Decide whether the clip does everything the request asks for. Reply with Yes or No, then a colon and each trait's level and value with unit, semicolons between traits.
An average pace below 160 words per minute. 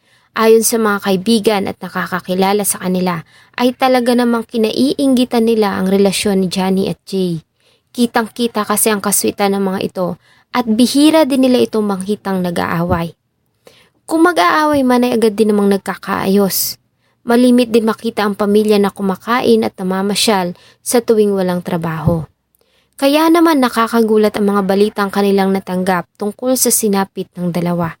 Yes: average, 145 wpm